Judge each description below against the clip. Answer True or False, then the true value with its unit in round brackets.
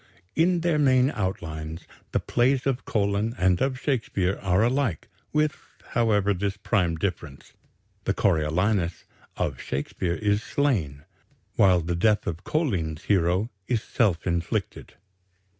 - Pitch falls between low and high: False (100 Hz)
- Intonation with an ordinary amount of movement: False (6.1 semitones)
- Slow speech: True (125 wpm)